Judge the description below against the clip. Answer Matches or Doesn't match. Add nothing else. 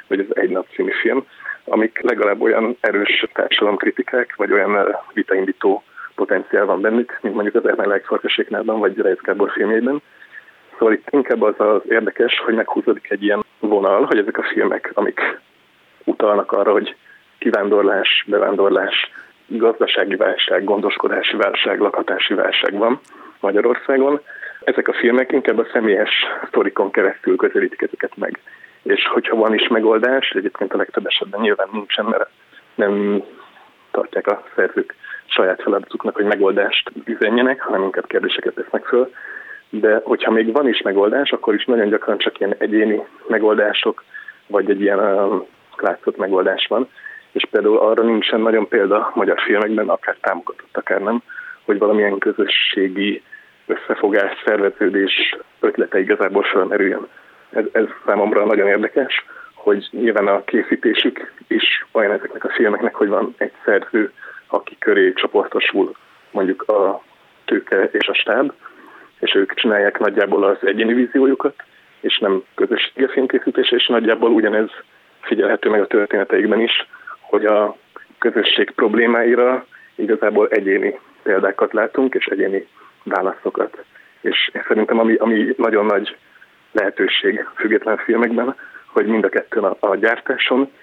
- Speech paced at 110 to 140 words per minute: Matches